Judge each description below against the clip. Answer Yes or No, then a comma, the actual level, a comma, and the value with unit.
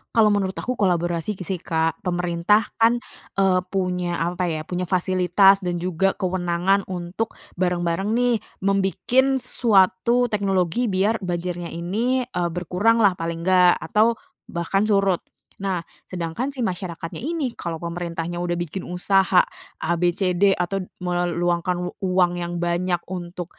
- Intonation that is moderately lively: No, narrow, 2.3 semitones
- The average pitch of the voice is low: No, medium, 180 Hz